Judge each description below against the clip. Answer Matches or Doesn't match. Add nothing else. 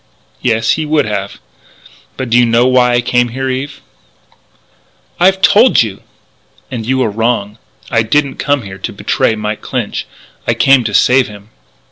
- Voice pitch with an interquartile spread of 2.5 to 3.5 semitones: Matches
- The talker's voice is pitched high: Doesn't match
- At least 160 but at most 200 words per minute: Matches